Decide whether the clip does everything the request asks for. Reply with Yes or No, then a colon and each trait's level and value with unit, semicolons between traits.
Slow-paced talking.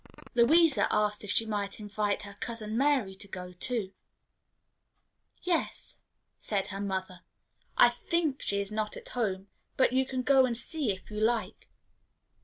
No: average, 155 wpm